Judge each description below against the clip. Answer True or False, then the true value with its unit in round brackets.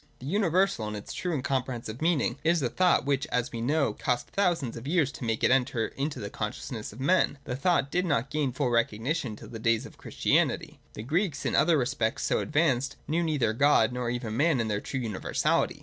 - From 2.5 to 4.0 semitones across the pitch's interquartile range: False (5.0 semitones)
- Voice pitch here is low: True (130 Hz)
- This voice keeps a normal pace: False (220 wpm)